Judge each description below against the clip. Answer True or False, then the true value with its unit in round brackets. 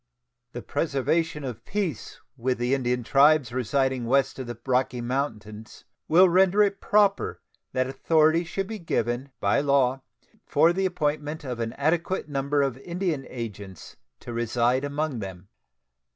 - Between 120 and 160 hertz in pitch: True (135 Hz)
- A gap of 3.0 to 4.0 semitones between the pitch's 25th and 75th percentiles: False (4.8 semitones)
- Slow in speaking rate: False (145 wpm)